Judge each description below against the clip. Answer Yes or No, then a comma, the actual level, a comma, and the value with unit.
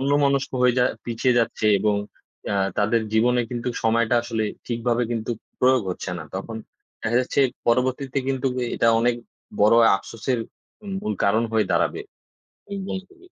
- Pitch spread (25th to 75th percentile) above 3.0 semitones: No, narrow, 2.5 semitones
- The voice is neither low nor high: No, low, 120 Hz